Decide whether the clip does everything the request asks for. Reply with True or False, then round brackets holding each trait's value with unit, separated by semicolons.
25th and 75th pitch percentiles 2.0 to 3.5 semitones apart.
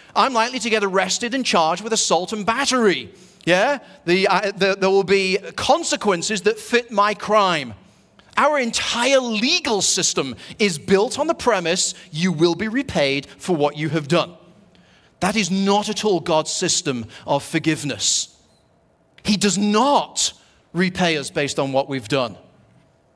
False (5.0 semitones)